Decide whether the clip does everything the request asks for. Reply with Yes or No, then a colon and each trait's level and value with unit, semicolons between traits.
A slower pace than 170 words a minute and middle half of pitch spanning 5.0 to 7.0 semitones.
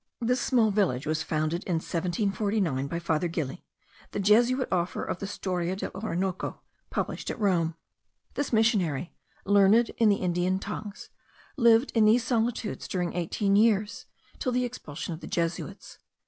No: average, 150 wpm; average, 4.5 semitones